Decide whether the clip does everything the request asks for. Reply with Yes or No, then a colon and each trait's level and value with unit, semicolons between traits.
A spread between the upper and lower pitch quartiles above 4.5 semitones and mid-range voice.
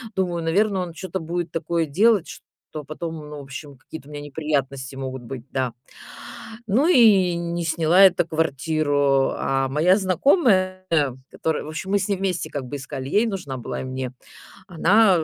Yes: average, 5.0 semitones; medium, 160 Hz